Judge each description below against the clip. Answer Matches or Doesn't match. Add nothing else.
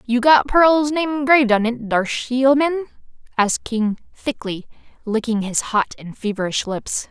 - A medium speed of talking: Matches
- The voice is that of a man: Doesn't match